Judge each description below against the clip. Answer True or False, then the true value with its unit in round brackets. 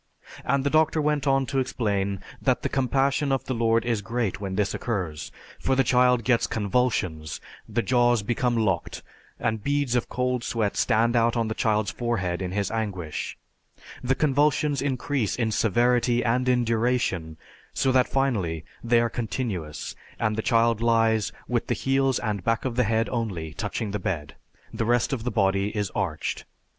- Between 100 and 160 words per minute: False (175 wpm)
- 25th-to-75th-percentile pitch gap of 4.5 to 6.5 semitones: False (3.8 semitones)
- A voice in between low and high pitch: False (115 Hz)